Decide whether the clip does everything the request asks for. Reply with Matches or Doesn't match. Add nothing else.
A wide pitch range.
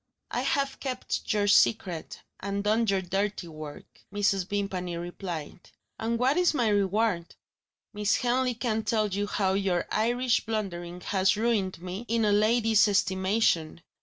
Doesn't match